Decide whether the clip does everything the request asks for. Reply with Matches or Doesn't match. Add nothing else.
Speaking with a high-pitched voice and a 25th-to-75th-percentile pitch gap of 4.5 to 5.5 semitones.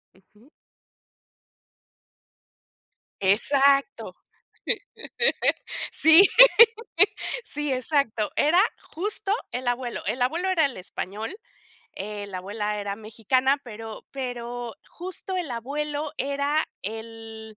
Matches